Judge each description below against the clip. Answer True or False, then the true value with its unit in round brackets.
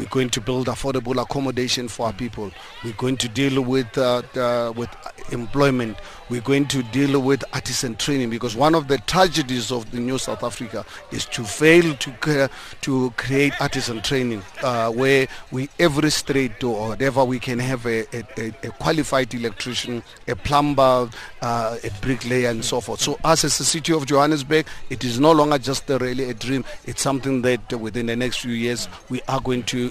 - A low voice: True (130 Hz)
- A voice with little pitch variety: True (2.3 semitones)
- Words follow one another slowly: False (190 wpm)